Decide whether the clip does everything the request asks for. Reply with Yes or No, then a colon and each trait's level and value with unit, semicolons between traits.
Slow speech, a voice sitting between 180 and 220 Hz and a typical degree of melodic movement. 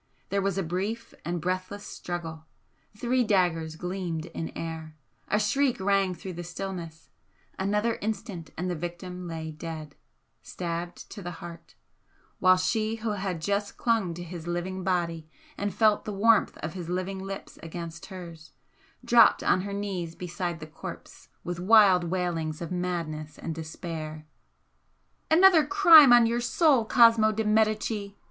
No: average, 150 wpm; medium, 185 Hz; average, 3.8 semitones